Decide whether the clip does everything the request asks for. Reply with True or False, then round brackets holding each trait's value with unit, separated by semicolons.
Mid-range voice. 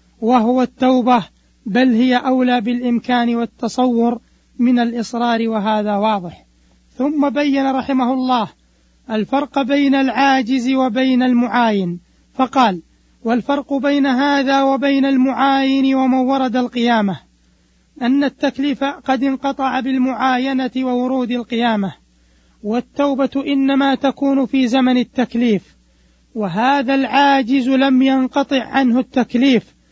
False (255 Hz)